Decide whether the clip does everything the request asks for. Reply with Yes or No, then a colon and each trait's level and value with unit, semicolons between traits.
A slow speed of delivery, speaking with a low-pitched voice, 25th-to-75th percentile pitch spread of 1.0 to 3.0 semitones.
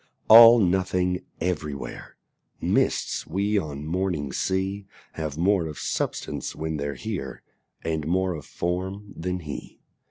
No: slow, 125 wpm; very low, 90 Hz; average, 3.7 semitones